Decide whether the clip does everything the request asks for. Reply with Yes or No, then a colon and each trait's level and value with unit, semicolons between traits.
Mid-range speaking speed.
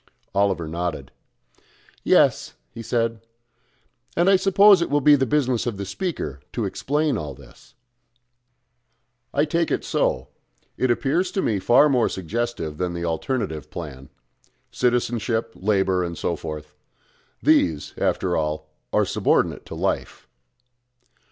No: slow, 130 wpm